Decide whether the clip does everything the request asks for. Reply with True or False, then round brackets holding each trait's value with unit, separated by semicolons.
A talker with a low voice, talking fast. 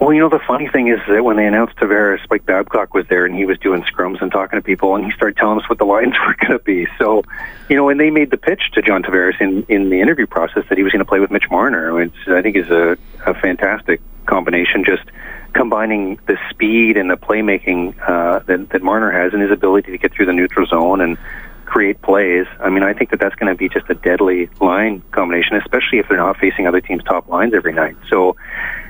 True (100 Hz; 250 wpm)